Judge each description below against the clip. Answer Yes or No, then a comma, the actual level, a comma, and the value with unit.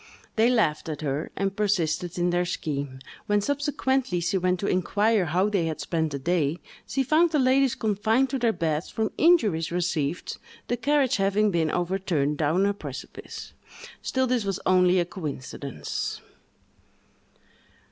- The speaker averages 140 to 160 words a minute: Yes, average, 155 wpm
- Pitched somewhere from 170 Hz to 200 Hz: Yes, medium, 185 Hz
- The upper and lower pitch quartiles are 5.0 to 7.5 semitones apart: Yes, wide, 5.5 semitones